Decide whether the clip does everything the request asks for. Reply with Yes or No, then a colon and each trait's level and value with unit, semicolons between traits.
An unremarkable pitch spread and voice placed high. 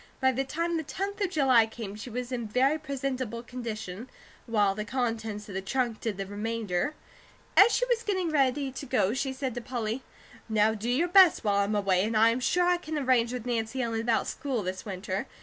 Yes: average, 4.1 semitones; high, 240 Hz